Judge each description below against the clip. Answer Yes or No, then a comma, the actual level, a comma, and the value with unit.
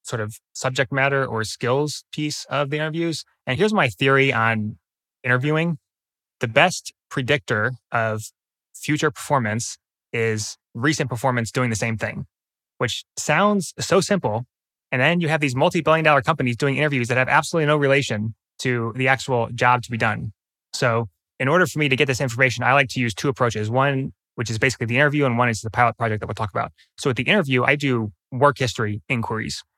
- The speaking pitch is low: Yes, low, 130 Hz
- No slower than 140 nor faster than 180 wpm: No, average, 195 wpm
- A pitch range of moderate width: Yes, average, 4.2 semitones